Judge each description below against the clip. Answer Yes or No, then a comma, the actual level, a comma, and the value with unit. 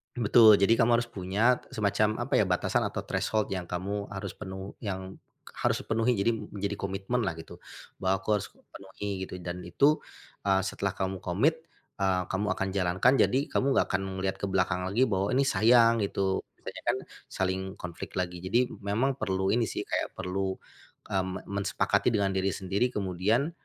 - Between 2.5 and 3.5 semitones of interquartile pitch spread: Yes, average, 3.1 semitones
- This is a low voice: Yes, very low, 95 Hz